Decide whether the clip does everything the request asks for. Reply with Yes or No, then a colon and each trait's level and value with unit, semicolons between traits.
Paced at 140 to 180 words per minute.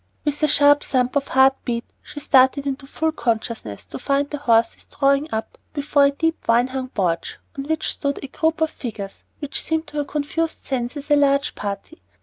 No: average, 195 wpm